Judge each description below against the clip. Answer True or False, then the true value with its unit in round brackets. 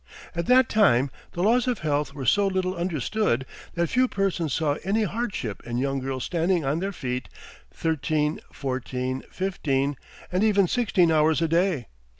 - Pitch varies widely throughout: True (6.2 semitones)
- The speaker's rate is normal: True (160 wpm)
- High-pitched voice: False (165 Hz)